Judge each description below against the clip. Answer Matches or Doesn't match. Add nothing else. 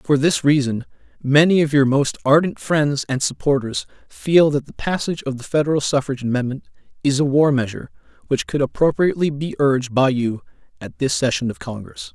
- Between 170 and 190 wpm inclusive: Matches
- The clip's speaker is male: Matches